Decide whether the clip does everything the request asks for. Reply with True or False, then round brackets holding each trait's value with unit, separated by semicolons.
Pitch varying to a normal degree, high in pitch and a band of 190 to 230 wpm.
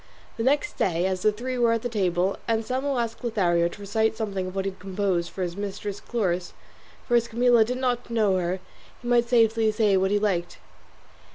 True (3.8 semitones; 215 Hz; 200 wpm)